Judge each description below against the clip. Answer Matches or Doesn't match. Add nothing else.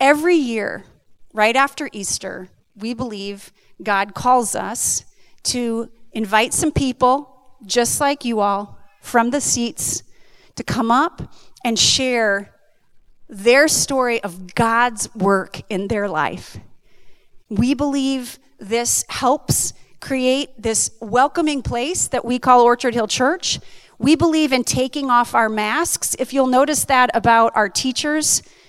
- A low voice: Doesn't match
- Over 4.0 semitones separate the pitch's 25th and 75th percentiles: Doesn't match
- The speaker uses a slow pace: Matches